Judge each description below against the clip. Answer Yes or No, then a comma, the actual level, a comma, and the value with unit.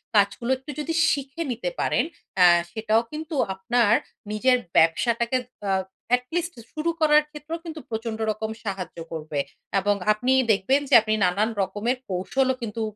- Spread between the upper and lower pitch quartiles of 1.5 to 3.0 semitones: No, wide, 5.4 semitones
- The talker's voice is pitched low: No, high, 230 Hz